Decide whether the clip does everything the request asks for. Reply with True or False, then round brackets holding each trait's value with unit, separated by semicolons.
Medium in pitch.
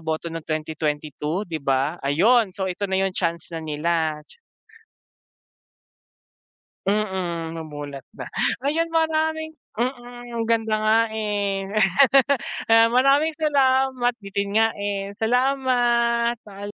False (205 Hz)